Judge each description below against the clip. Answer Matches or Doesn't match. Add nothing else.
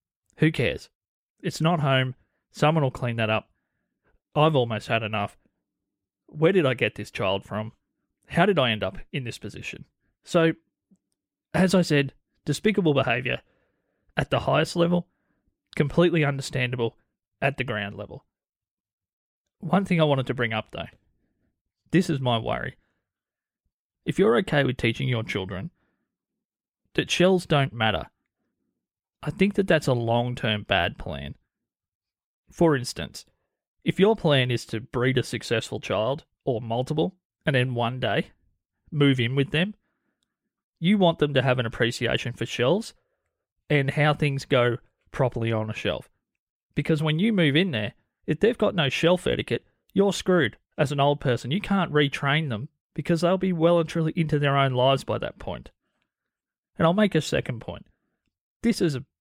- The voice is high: Doesn't match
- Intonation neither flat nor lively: Doesn't match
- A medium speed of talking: Matches